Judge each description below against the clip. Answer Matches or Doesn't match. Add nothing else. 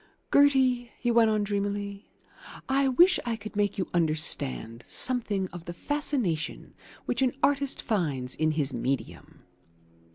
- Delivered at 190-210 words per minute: Doesn't match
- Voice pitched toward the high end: Matches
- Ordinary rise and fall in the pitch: Doesn't match